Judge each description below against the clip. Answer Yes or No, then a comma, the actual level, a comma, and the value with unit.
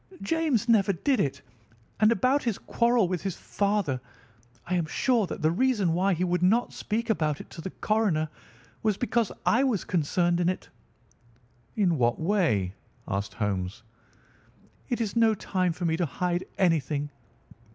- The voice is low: No, medium, 185 Hz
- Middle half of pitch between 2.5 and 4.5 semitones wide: No, wide, 5.5 semitones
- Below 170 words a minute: Yes, average, 160 wpm